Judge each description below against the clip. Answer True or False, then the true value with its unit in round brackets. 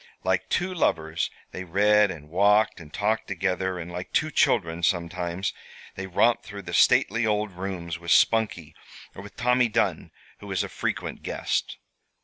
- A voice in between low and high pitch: False (95 Hz)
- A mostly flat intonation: False (3.5 semitones)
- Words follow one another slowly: False (160 wpm)